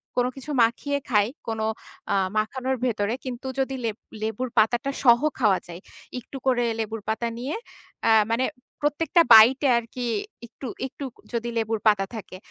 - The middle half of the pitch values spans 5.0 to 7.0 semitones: No, average, 3.1 semitones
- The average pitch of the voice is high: Yes, high, 235 Hz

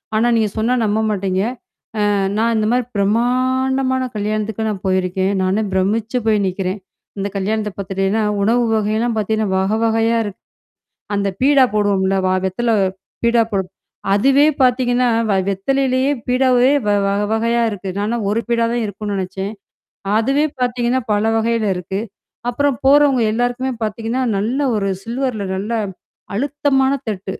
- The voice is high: Yes, high, 220 Hz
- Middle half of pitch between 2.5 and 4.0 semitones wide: Yes, average, 3.7 semitones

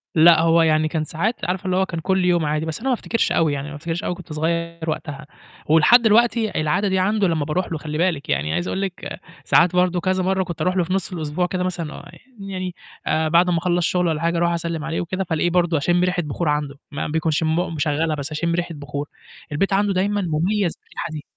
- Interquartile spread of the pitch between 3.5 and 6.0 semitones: No, average, 2.9 semitones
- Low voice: No, medium, 170 Hz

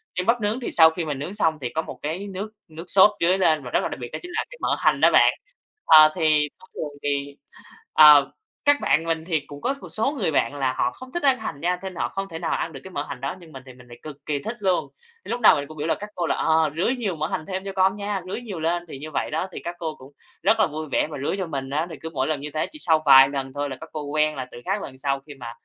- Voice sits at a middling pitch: Yes, medium, 160 Hz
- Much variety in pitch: No, average, 4.8 semitones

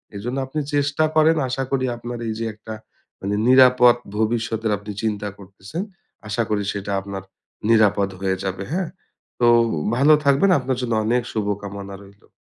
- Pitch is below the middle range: Yes, low, 110 Hz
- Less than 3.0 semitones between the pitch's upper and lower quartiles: No, average, 4.3 semitones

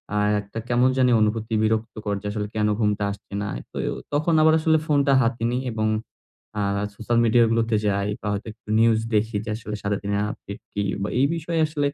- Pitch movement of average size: Yes, average, 3.3 semitones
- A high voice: No, low, 110 Hz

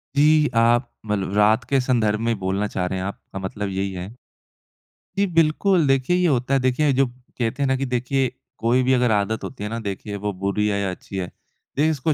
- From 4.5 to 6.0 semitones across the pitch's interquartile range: Yes, average, 4.9 semitones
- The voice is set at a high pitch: No, low, 120 Hz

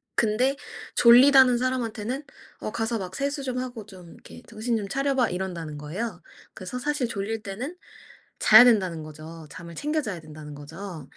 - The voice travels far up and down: Yes, wide, 6.7 semitones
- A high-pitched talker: Yes, high, 220 Hz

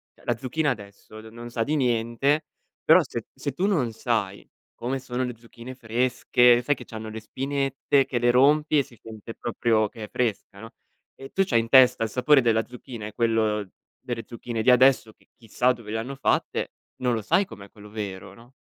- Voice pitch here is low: Yes, low, 120 Hz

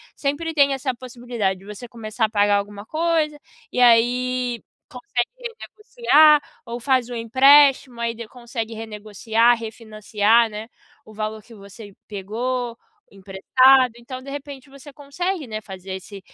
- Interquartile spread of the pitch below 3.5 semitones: No, average, 3.9 semitones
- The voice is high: Yes, high, 235 Hz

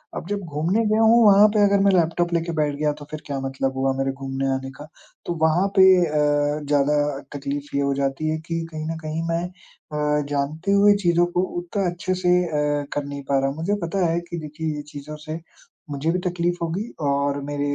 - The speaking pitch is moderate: Yes, medium, 155 Hz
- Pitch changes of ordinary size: Yes, average, 3.5 semitones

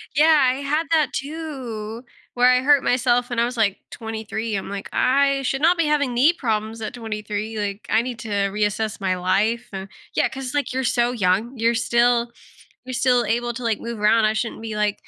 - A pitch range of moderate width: Yes, average, 3.2 semitones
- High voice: Yes, high, 235 Hz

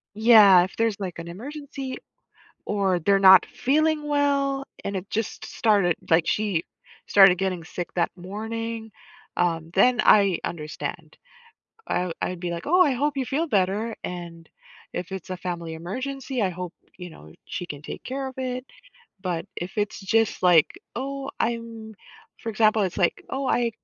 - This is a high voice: Yes, high, 205 Hz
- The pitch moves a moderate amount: No, wide, 6.0 semitones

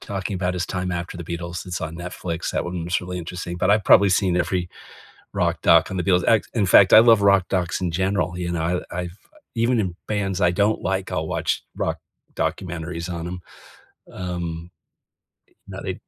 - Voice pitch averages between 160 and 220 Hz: No, very low, 90 Hz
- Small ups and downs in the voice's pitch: Yes, narrow, 1.7 semitones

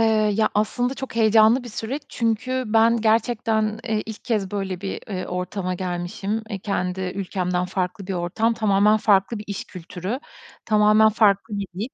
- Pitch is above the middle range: Yes, high, 210 Hz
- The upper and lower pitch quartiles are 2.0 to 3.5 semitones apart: Yes, average, 2.8 semitones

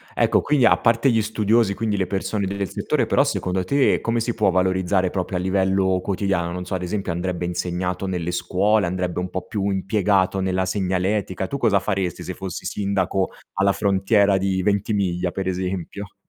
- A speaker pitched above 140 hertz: No, very low, 95 Hz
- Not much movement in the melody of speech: Yes, narrow, 1.8 semitones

